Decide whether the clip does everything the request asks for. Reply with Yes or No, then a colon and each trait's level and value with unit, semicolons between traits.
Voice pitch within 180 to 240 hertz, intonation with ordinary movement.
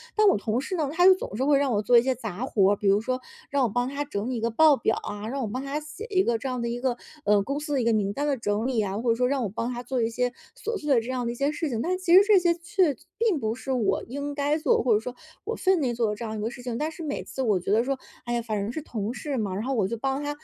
No: very high, 250 Hz; average, 4.5 semitones